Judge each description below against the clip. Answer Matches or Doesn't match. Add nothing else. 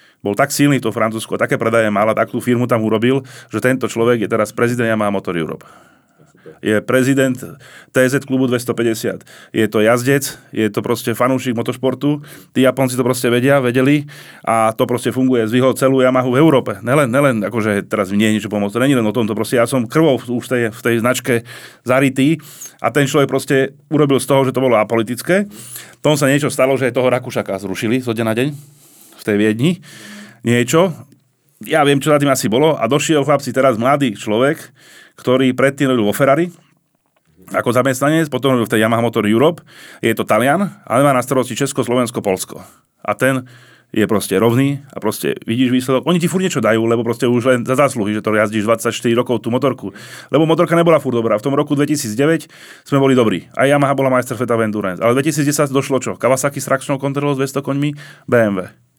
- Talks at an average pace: Doesn't match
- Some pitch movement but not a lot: Matches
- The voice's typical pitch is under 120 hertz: Doesn't match